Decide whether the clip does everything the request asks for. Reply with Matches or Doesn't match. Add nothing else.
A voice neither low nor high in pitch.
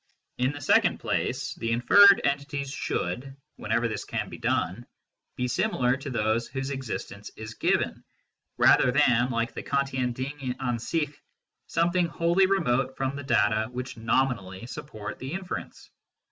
Doesn't match